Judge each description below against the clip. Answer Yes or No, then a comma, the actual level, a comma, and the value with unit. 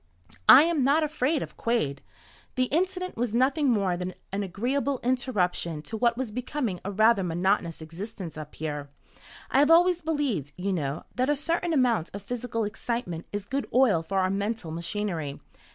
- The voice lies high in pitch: Yes, high, 220 Hz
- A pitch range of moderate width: No, wide, 6.9 semitones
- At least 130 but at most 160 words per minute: No, average, 170 wpm